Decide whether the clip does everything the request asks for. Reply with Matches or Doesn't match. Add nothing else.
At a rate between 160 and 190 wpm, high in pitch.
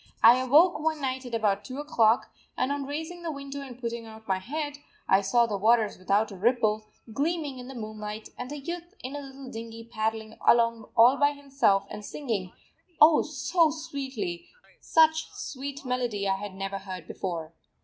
Matches